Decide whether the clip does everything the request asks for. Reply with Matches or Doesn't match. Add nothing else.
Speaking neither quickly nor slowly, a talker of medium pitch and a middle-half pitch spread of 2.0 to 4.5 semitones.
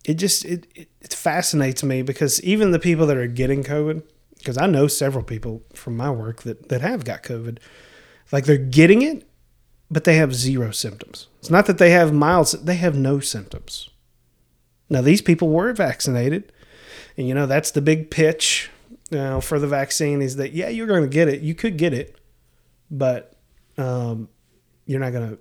Doesn't match